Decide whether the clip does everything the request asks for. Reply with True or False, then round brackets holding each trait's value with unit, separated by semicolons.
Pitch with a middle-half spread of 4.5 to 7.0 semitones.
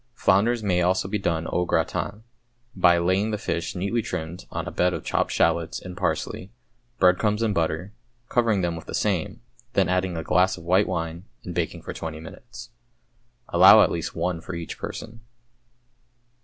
False (3.3 semitones)